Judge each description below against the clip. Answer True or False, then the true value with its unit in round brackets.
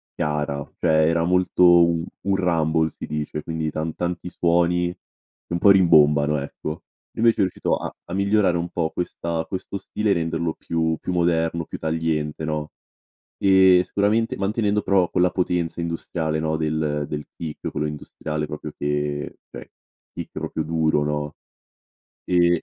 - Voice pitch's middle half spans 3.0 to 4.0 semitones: False (2.4 semitones)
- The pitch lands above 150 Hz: False (80 Hz)